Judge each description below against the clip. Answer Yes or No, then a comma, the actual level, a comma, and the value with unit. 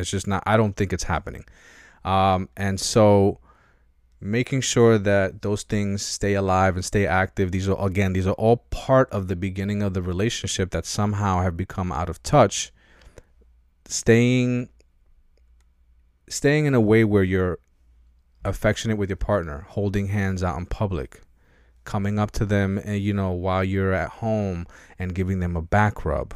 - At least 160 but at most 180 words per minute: Yes, average, 170 wpm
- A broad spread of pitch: No, average, 2.7 semitones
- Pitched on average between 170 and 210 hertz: No, very low, 95 Hz